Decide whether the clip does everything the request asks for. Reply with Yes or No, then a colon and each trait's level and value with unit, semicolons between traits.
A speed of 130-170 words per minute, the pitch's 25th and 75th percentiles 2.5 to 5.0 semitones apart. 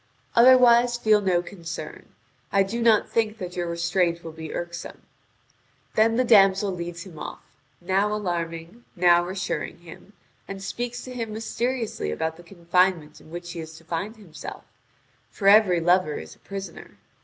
Yes: average, 160 wpm; average, 4.1 semitones